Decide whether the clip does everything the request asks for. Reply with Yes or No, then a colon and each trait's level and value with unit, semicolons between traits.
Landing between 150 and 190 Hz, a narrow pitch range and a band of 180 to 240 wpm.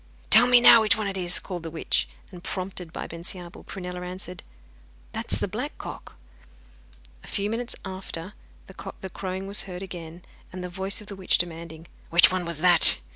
Yes: medium, 185 Hz; narrow, 2.0 semitones; average, 185 wpm